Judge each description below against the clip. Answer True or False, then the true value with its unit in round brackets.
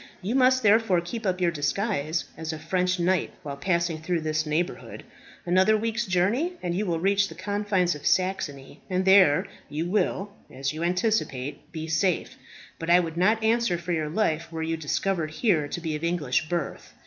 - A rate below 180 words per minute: False (185 wpm)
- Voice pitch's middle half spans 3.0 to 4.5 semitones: True (3.9 semitones)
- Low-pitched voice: False (175 Hz)